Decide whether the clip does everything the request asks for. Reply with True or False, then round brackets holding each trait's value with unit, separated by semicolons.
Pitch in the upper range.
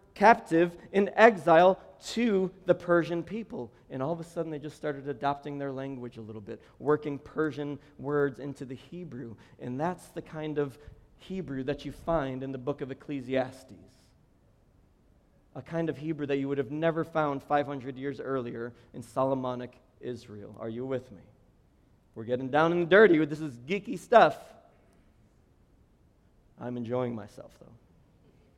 False (140 Hz)